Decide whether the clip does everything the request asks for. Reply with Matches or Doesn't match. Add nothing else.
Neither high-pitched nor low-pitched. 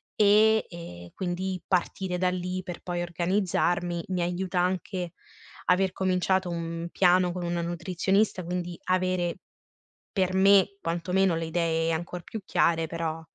Matches